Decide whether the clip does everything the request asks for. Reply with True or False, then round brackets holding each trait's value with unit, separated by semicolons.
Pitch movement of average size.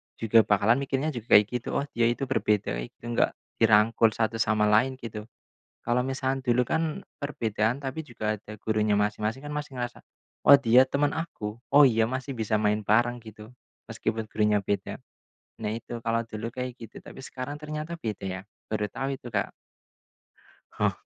True (3.6 semitones)